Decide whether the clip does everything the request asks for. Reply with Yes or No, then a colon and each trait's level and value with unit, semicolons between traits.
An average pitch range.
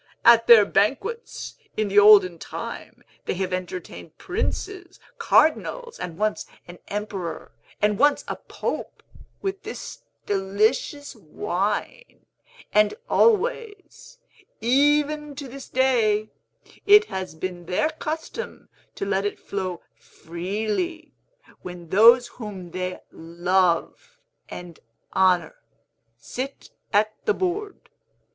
No: wide, 8.6 semitones